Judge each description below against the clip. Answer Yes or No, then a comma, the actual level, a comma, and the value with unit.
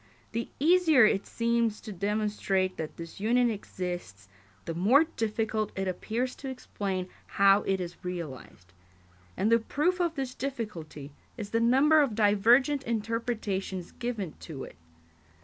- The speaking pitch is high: Yes, high, 215 Hz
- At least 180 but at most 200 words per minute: No, average, 140 wpm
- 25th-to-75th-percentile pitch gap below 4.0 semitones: No, average, 4.6 semitones